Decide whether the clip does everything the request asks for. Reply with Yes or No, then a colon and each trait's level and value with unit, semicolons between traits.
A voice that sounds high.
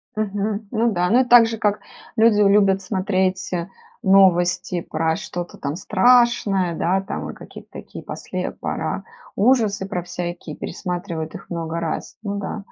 Yes: high, 195 Hz